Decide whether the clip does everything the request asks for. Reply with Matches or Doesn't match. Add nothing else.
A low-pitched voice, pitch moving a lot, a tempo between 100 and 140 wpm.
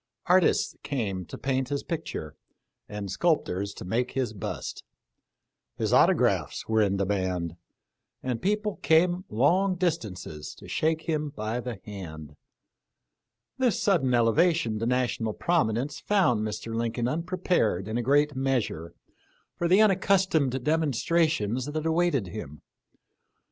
Matches